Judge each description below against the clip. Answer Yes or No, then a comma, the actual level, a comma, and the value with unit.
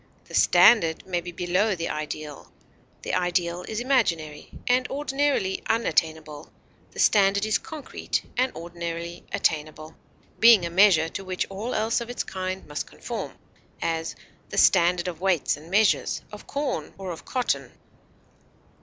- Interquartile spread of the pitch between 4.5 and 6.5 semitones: Yes, average, 4.9 semitones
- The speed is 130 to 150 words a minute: Yes, average, 145 wpm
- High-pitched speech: No, medium, 180 Hz